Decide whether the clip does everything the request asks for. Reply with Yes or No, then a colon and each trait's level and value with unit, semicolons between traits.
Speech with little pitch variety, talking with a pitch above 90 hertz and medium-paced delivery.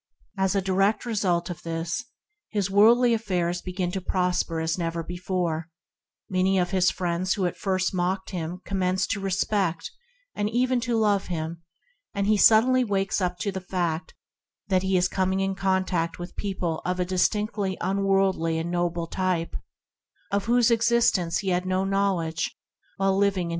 Yes: narrow, 2.2 semitones; medium, 185 Hz; average, 155 wpm